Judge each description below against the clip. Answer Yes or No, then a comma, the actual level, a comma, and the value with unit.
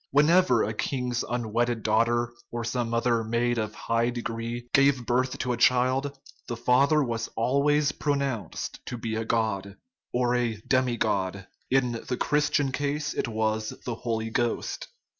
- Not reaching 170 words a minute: Yes, average, 160 wpm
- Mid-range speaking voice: No, low, 120 Hz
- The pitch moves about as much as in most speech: No, narrow, 2.3 semitones